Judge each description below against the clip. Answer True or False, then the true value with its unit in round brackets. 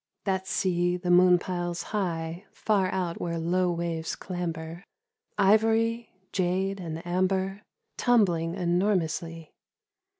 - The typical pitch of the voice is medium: True (180 Hz)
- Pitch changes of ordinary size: False (2.2 semitones)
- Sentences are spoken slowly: True (105 wpm)